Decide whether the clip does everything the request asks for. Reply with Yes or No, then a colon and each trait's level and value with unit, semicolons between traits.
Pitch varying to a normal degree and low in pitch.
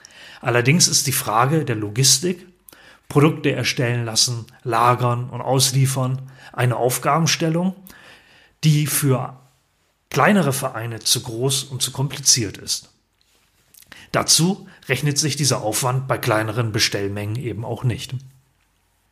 Yes: average, 3.3 semitones; low, 130 Hz